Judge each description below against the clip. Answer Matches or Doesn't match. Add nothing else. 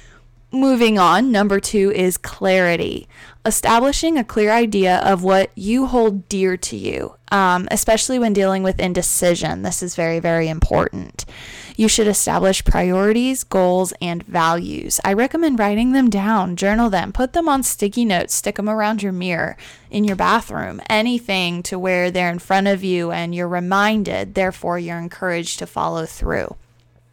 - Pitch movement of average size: Matches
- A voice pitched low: Doesn't match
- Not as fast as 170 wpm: Matches